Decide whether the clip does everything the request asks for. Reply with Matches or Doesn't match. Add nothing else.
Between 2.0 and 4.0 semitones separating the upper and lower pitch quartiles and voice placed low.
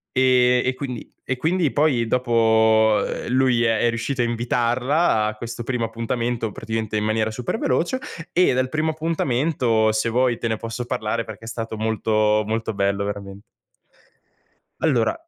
Matches